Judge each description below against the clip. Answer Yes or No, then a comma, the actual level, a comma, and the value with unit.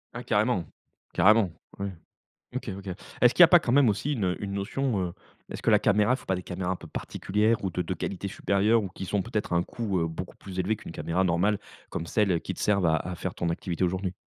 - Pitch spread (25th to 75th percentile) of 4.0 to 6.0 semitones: No, average, 3.0 semitones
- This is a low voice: Yes, low, 100 Hz